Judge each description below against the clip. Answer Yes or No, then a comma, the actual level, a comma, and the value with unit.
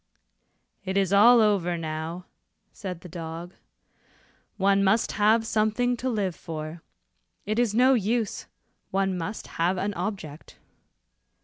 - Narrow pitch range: No, average, 3.9 semitones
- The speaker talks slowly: Yes, slow, 125 wpm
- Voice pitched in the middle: No, high, 195 Hz